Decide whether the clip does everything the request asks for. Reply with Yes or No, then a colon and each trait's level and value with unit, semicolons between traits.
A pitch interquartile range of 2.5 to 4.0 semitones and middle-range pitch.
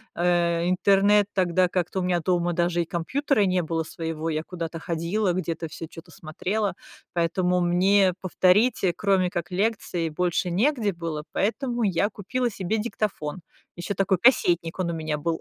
Yes: average, 2.9 semitones; medium, 180 Hz